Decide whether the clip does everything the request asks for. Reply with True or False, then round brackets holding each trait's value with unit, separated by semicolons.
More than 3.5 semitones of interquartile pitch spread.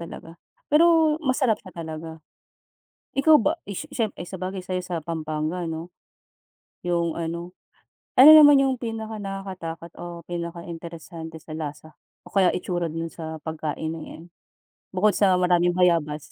False (3.2 semitones)